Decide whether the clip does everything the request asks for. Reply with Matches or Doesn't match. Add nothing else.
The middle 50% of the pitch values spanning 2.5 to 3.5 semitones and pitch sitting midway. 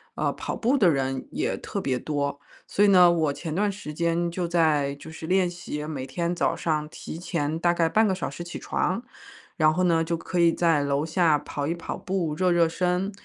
Matches